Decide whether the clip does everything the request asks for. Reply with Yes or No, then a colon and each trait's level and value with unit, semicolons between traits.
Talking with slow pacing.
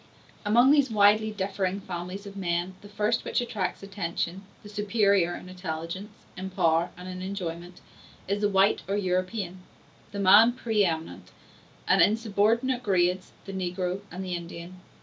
No: average, 155 wpm